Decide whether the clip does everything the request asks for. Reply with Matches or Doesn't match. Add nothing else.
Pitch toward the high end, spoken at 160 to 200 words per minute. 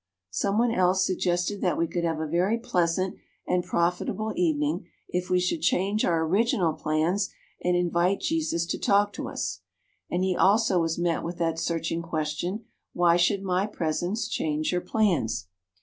Doesn't match